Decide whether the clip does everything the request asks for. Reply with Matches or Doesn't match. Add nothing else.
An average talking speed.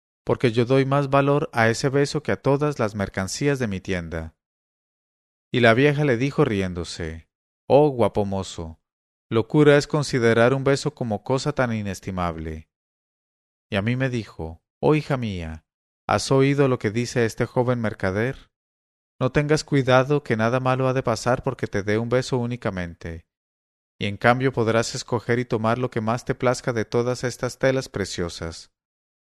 Matches